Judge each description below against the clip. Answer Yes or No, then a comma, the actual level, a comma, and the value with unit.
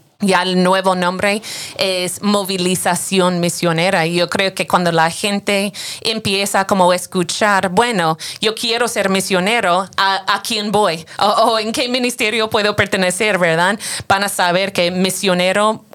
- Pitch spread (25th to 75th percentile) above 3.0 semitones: No, narrow, 2.5 semitones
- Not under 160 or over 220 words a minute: No, average, 150 wpm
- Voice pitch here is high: Yes, high, 195 Hz